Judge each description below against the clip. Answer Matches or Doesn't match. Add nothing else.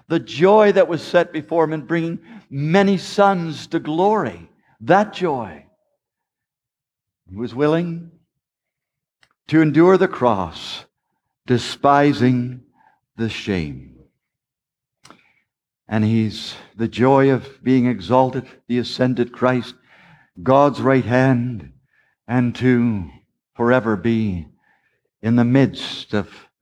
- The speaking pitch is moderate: Doesn't match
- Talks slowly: Matches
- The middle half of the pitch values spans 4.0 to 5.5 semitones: Matches